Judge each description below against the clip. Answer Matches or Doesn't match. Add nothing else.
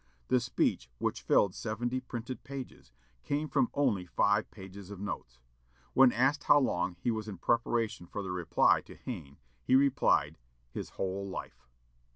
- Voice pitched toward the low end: Matches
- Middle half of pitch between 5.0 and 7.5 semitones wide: Matches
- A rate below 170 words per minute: Matches